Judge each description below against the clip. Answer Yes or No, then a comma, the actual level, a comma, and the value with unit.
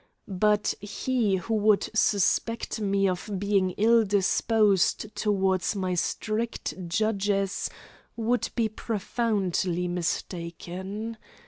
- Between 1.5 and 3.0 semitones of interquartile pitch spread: Yes, average, 2.7 semitones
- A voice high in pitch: Yes, high, 205 Hz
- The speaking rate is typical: No, slow, 95 wpm